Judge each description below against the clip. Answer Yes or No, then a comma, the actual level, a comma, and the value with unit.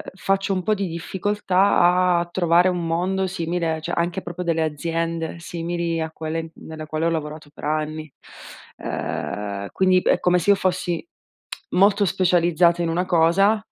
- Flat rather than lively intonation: Yes, narrow, 2.3 semitones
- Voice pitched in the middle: Yes, medium, 170 Hz